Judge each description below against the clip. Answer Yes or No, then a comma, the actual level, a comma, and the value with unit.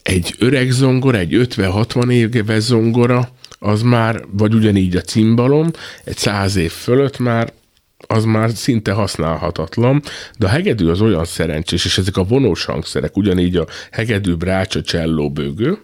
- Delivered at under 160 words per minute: Yes, average, 150 wpm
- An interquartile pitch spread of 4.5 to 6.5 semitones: Yes, average, 5.3 semitones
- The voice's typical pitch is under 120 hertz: Yes, low, 110 Hz